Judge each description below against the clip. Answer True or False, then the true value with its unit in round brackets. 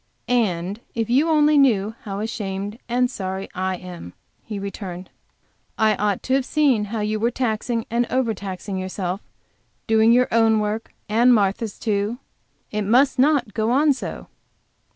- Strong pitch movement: False (3.6 semitones)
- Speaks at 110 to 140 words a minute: False (150 wpm)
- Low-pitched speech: False (220 Hz)